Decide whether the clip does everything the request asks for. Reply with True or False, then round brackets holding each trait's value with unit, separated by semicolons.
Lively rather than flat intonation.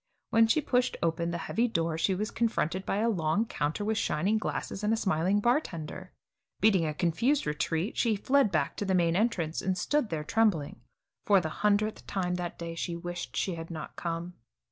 False (4.7 semitones)